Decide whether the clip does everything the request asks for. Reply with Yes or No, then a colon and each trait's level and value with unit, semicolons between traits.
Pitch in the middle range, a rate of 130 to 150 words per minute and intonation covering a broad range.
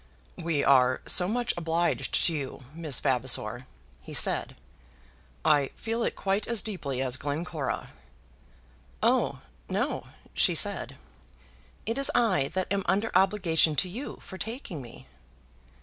Yes: medium, 170 Hz; slow, 135 wpm; wide, 6.6 semitones